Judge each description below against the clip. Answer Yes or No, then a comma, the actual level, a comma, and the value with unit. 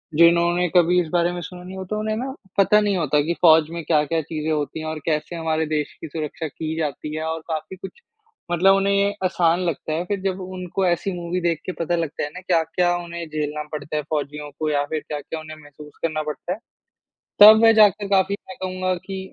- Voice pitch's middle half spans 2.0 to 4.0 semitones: Yes, average, 3.0 semitones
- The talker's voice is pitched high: No, medium, 170 Hz